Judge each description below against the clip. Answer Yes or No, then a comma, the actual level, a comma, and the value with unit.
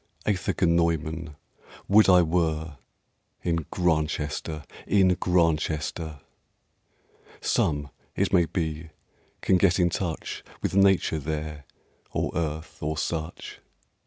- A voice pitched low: Yes, very low, 80 Hz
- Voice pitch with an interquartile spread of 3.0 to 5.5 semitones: No, narrow, 2.4 semitones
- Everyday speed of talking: No, slow, 105 wpm